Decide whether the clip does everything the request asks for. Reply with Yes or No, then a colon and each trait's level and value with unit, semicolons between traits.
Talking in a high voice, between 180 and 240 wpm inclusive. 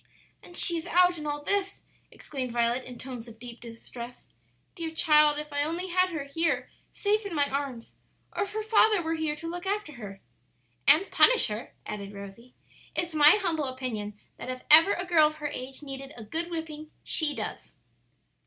Yes: very high, 300 Hz; average, 190 wpm